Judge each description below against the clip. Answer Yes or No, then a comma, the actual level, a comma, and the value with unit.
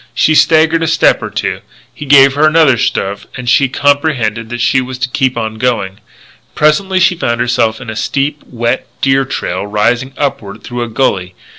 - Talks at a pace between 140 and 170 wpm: No, average, 185 wpm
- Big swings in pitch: No, average, 4.0 semitones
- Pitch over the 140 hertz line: No, low, 125 Hz